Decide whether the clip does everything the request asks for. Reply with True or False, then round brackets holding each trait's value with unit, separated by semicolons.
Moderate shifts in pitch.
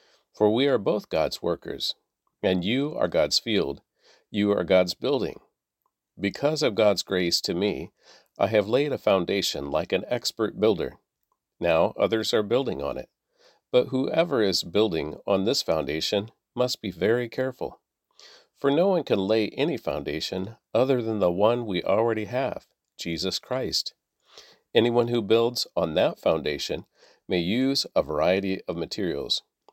True (4.5 semitones)